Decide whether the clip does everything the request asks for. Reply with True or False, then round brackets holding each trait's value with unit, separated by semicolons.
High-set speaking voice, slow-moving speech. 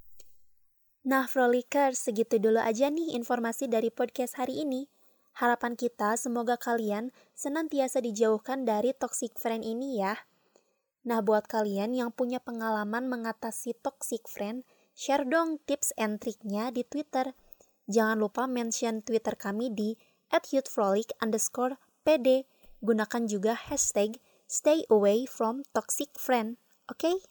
False (245 Hz; 115 wpm)